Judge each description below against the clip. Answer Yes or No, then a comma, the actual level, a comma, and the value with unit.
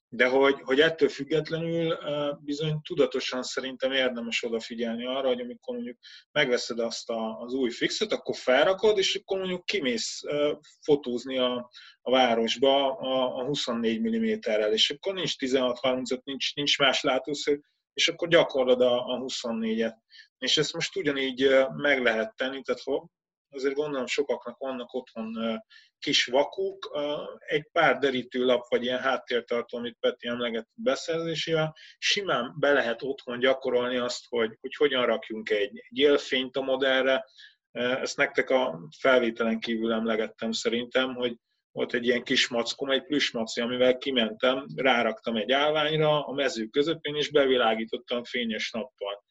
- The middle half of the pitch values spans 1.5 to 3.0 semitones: No, average, 3.6 semitones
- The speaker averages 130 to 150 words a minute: Yes, average, 135 wpm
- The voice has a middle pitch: No, low, 130 Hz